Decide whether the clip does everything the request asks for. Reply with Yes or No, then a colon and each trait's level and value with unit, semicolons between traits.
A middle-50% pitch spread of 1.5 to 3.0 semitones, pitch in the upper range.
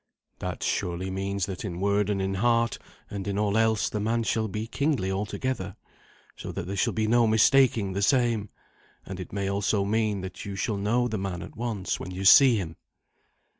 No: average, 2.7 semitones; low, 100 Hz